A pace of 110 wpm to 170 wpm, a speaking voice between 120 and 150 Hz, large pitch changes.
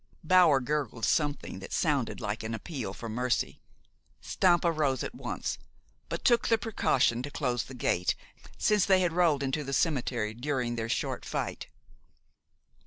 Yes: average, 155 wpm; medium, 140 Hz; wide, 5.9 semitones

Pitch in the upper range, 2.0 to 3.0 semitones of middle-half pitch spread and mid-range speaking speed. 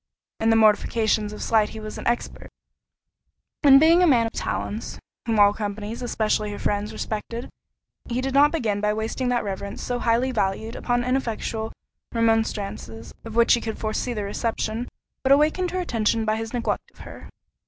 Yes: high, 225 Hz; narrow, 2.5 semitones; average, 175 wpm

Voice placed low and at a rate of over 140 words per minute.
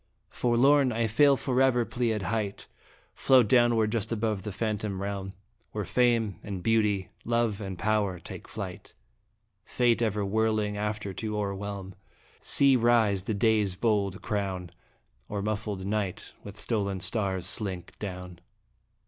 No: low, 105 Hz; slow, 135 wpm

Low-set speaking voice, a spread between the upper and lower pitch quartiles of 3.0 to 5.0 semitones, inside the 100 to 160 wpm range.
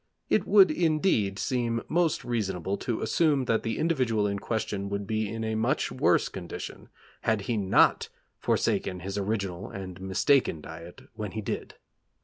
Yes: low, 110 Hz; average, 3.8 semitones; average, 155 wpm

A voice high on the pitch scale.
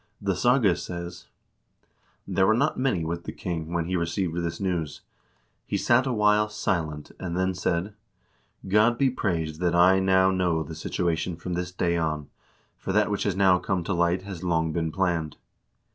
No: very low, 90 Hz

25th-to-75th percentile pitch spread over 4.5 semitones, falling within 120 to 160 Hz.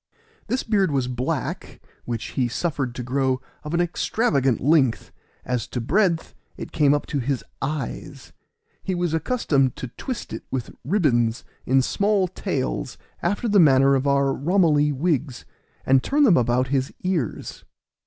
Yes: average, 5.3 semitones; medium, 140 Hz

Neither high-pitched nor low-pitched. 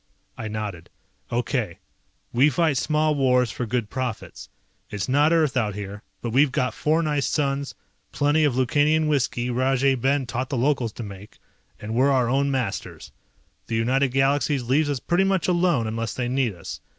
No: low, 130 Hz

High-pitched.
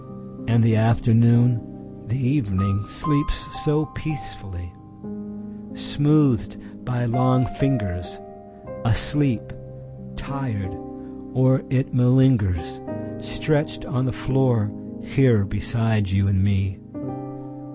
No: low, 120 Hz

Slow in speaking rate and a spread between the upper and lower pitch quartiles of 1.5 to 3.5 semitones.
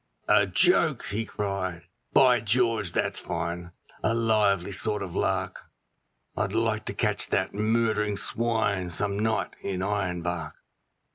Yes: slow, 130 wpm; average, 3.2 semitones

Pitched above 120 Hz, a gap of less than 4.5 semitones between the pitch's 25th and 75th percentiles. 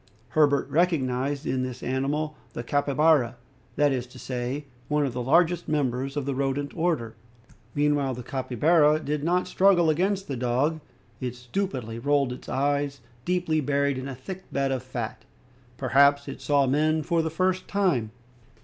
Yes: medium, 140 Hz; average, 3.3 semitones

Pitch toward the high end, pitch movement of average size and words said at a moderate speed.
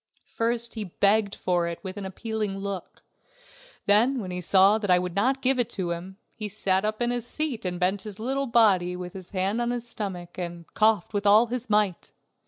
No: high, 205 Hz; average, 3.7 semitones; fast, 210 wpm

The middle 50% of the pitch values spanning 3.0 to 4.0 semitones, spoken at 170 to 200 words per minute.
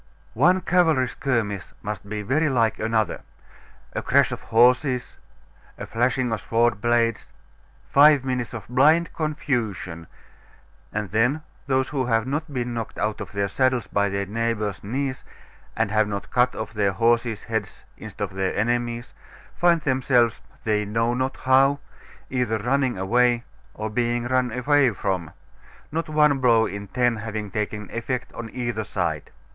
No: average, 3.4 semitones; average, 155 wpm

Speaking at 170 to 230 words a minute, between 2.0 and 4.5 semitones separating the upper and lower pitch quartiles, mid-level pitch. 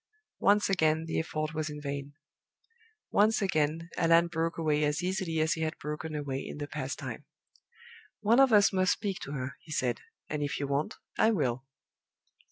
Yes: average, 180 wpm; average, 3.5 semitones; medium, 155 Hz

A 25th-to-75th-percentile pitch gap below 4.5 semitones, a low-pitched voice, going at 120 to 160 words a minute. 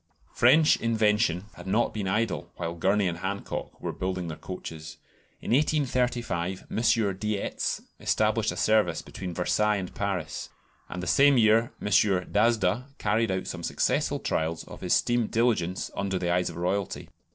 Yes: average, 4.0 semitones; low, 100 Hz; average, 155 wpm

